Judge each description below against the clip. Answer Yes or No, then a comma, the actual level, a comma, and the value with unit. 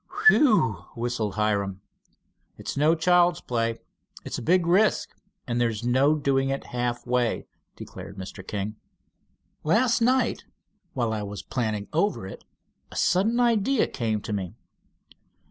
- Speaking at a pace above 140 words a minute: No, slow, 135 wpm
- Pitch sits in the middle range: No, low, 120 Hz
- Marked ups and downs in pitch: Yes, wide, 8.7 semitones